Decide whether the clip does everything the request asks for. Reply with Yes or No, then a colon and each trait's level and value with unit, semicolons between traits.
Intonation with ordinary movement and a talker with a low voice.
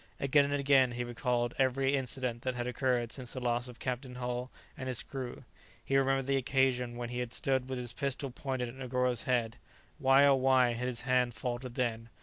No: narrow, 1.6 semitones; low, 125 Hz